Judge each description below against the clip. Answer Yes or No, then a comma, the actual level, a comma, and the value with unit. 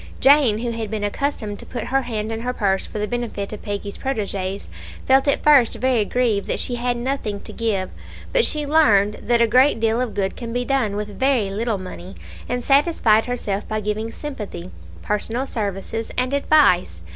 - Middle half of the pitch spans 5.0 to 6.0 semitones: No, average, 3.7 semitones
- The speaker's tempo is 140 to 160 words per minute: No, average, 190 wpm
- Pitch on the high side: Yes, high, 225 Hz